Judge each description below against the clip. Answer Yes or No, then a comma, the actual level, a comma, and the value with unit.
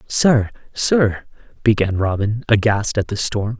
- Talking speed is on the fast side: No, slow, 135 wpm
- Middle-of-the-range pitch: No, low, 110 Hz